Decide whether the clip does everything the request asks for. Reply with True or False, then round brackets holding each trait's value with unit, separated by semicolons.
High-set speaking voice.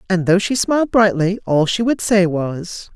True (195 Hz)